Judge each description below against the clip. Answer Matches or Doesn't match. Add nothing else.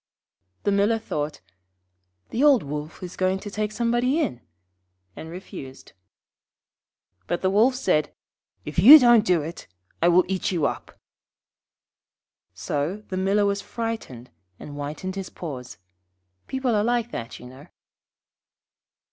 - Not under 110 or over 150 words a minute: Matches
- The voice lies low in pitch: Doesn't match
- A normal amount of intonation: Doesn't match